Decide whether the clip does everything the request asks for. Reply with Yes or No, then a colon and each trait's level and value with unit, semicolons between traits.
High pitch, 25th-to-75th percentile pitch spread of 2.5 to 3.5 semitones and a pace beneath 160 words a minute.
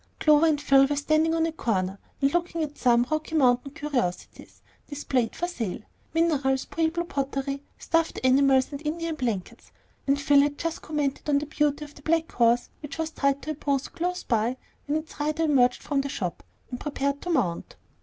No: very high, 285 Hz; average, 2.9 semitones; average, 185 wpm